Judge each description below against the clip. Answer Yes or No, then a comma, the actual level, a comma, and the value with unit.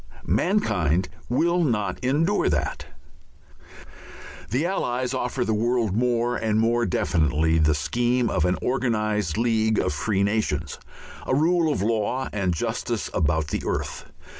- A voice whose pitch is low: Yes, low, 110 Hz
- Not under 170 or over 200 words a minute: No, slow, 135 wpm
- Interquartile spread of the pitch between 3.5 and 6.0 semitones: Yes, wide, 5.5 semitones